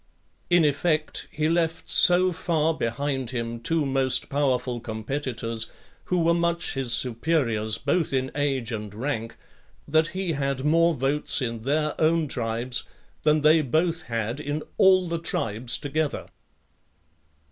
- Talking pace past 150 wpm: No, slow, 135 wpm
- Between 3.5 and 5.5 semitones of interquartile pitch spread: Yes, average, 5.1 semitones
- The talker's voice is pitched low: No, medium, 145 Hz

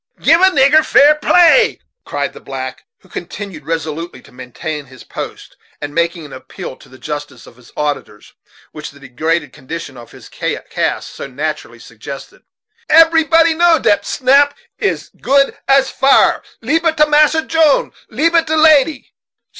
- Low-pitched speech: No, high, 220 Hz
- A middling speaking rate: Yes, average, 160 wpm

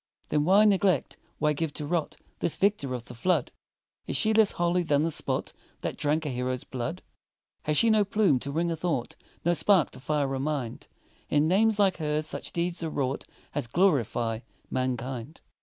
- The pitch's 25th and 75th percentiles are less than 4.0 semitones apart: No, average, 5.1 semitones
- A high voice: No, medium, 155 Hz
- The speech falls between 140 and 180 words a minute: No, average, 190 wpm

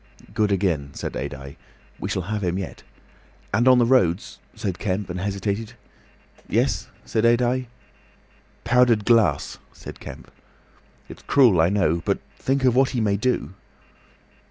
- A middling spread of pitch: Yes, average, 4.9 semitones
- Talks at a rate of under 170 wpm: Yes, average, 145 wpm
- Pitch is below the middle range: Yes, low, 105 Hz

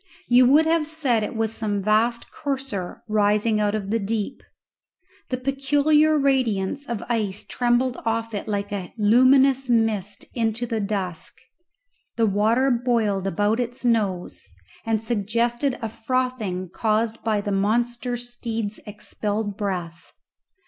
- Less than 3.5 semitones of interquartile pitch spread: Yes, average, 3.1 semitones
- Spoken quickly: No, slow, 135 wpm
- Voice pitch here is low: No, high, 225 Hz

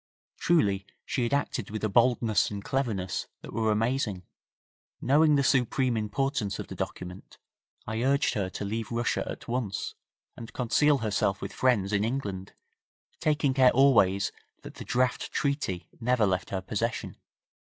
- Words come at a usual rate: Yes, average, 150 wpm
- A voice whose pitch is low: Yes, low, 115 Hz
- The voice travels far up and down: No, average, 4.7 semitones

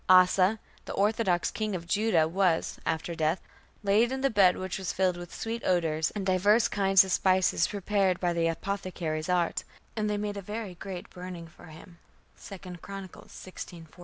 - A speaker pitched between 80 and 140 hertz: No, medium, 185 Hz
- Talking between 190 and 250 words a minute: No, average, 180 wpm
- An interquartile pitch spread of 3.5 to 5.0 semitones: No, narrow, 2.6 semitones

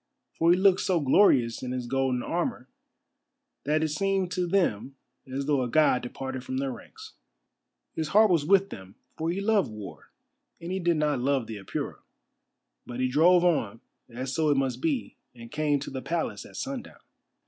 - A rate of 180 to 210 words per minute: Yes, average, 185 wpm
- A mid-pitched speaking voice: Yes, medium, 150 Hz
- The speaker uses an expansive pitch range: Yes, wide, 5.7 semitones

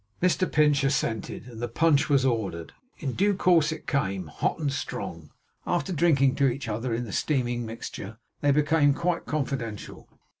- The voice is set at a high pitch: No, low, 135 Hz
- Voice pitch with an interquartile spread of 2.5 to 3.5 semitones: No, average, 5.0 semitones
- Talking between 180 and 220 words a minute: No, average, 165 wpm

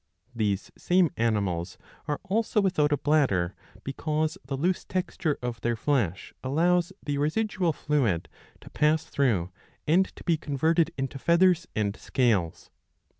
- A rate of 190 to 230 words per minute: No, slow, 135 wpm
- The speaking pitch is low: No, medium, 145 Hz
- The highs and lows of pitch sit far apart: Yes, wide, 6.4 semitones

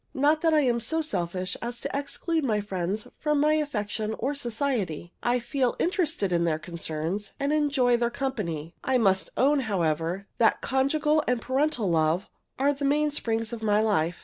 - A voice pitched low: No, high, 235 Hz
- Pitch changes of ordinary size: No, wide, 7.0 semitones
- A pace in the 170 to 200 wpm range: Yes, average, 175 wpm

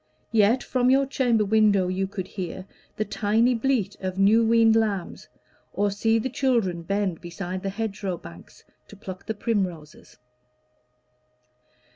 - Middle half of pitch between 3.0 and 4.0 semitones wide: Yes, average, 3.3 semitones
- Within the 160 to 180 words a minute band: No, average, 140 wpm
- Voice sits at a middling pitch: No, high, 205 Hz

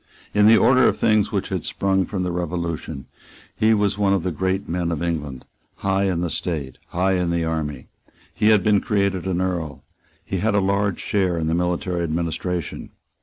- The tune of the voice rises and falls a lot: No, average, 2.7 semitones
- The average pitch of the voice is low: Yes, very low, 90 Hz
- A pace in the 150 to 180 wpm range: No, average, 195 wpm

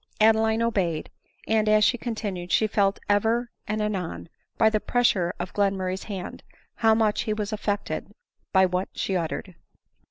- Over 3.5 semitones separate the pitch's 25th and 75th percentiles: No, average, 2.7 semitones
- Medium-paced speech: Yes, average, 155 wpm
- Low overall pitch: No, high, 210 Hz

